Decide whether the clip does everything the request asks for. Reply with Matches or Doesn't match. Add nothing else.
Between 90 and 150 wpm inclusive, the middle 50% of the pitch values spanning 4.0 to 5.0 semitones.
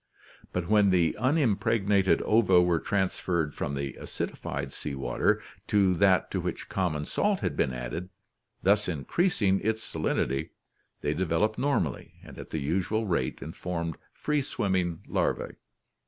Matches